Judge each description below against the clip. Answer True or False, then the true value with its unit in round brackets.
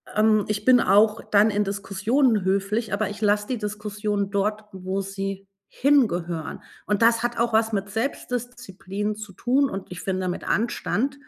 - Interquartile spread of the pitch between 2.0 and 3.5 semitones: True (2.6 semitones)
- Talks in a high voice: True (210 Hz)